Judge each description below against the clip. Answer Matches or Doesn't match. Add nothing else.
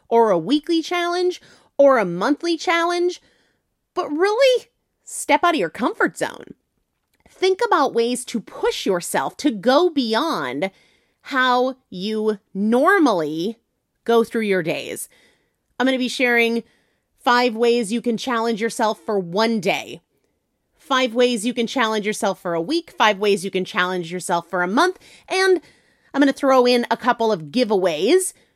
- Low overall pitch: Doesn't match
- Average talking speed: Matches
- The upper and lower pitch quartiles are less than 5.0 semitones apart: Doesn't match